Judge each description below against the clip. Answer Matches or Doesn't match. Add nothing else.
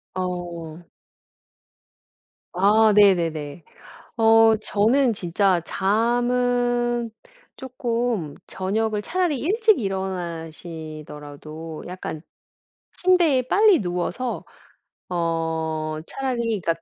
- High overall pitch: Matches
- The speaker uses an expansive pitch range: Matches